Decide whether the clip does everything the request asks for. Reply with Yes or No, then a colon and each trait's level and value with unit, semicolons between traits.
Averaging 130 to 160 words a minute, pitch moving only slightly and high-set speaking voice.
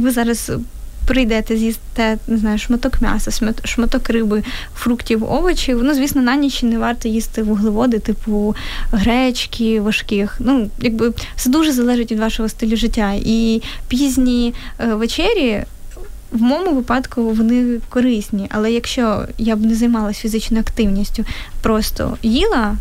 Yes: average, 135 wpm; narrow, 1.8 semitones; high, 230 Hz